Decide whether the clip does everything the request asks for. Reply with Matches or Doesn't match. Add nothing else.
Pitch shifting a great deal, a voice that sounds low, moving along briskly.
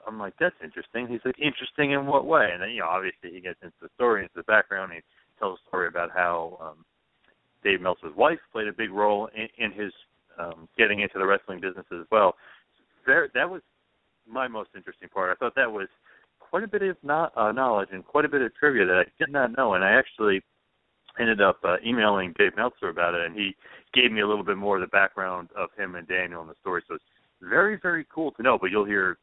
Matches